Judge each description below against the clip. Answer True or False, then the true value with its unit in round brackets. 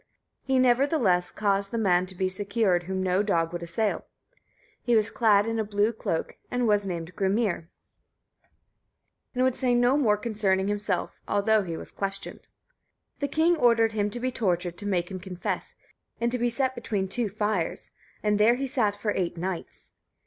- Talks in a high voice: True (205 Hz)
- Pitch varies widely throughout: False (4.0 semitones)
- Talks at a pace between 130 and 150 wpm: False (180 wpm)